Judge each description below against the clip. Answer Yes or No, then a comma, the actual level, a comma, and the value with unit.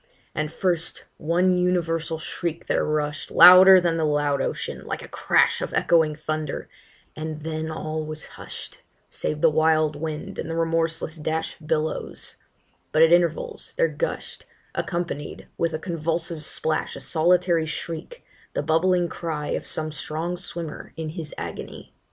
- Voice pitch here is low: No, medium, 160 Hz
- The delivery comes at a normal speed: Yes, average, 150 wpm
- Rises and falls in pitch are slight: Yes, narrow, 1.7 semitones